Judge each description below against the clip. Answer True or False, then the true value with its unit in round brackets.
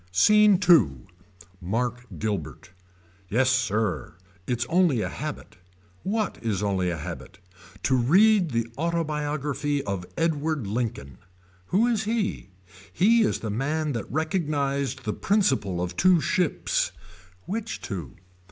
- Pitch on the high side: False (140 Hz)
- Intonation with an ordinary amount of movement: False (8.7 semitones)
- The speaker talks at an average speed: False (125 wpm)